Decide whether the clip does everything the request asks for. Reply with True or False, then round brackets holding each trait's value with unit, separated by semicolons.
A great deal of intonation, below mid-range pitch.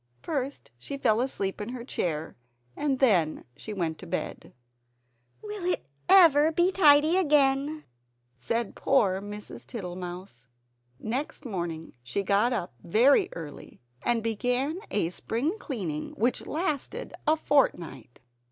False (8.0 semitones; 235 Hz)